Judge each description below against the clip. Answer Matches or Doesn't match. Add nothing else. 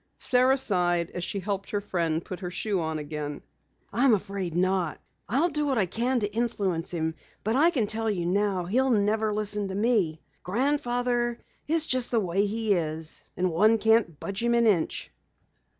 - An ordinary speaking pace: Matches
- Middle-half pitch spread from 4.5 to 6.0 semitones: Matches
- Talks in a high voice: Matches